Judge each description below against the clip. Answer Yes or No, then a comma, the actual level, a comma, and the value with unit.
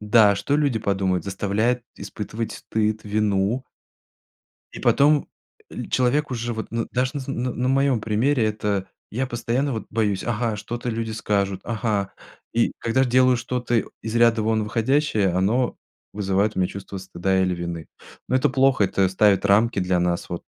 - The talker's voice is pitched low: Yes, low, 110 Hz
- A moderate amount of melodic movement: Yes, average, 3.8 semitones